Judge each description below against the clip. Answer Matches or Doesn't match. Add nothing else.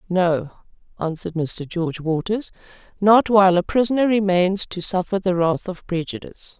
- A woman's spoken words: Matches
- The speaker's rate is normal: Matches